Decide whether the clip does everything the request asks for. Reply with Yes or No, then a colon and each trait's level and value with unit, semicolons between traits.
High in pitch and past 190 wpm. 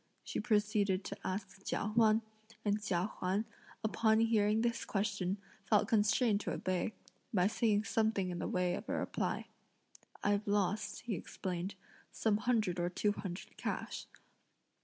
No: high, 205 Hz; average, 145 wpm